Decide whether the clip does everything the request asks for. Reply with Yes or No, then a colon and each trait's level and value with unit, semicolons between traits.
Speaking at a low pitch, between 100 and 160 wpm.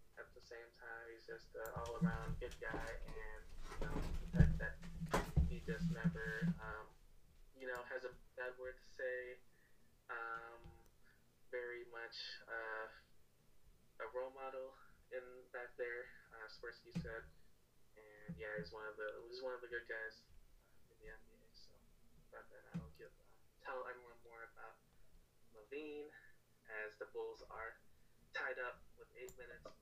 Yes: low, 120 Hz; average, 150 wpm